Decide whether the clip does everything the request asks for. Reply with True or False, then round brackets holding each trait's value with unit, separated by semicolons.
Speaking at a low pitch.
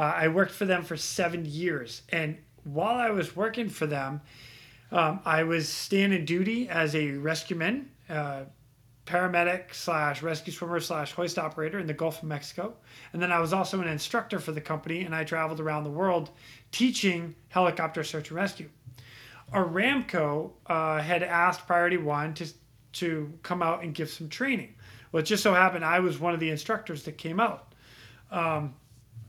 False (165 Hz)